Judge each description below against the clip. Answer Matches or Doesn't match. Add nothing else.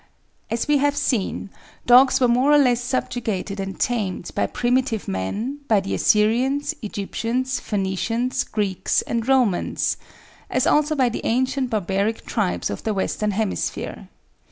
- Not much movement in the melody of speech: Doesn't match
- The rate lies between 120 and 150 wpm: Matches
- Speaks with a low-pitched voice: Doesn't match